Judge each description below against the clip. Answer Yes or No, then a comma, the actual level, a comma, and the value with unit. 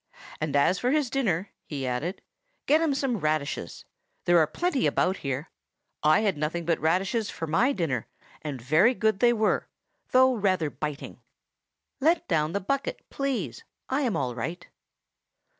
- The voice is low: No, medium, 180 Hz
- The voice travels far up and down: Yes, wide, 8.2 semitones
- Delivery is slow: No, average, 160 wpm